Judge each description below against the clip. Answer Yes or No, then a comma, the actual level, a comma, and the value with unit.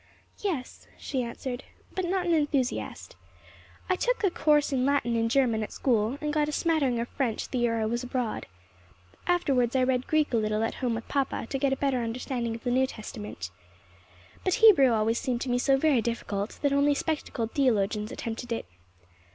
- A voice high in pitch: Yes, very high, 255 Hz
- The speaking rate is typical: Yes, average, 190 wpm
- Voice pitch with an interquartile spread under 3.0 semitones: No, average, 3.8 semitones